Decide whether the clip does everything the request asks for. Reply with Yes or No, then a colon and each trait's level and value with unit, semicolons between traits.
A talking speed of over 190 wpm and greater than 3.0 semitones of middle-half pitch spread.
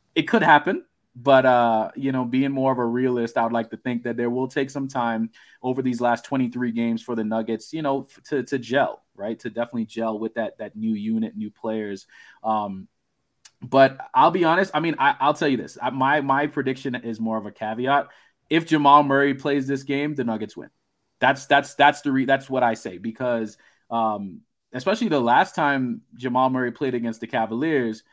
Yes: fast, 205 wpm; average, 3.5 semitones